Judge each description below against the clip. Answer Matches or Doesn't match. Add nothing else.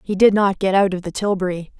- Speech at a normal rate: Doesn't match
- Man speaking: Doesn't match